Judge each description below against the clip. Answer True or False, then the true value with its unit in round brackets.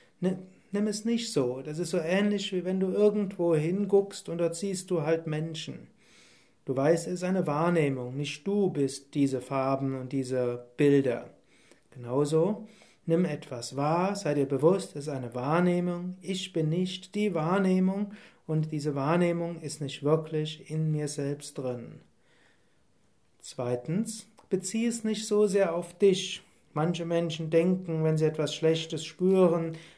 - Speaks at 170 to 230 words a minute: False (150 wpm)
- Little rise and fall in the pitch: False (4.3 semitones)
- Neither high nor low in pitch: True (165 Hz)